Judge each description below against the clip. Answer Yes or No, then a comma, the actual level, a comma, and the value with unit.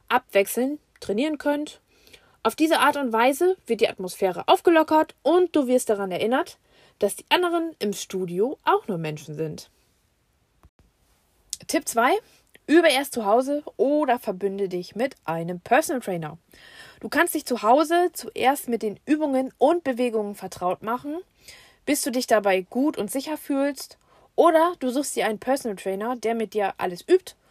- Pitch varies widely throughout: Yes, wide, 7.0 semitones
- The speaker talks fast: No, average, 155 wpm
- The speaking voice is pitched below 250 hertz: No, very high, 255 Hz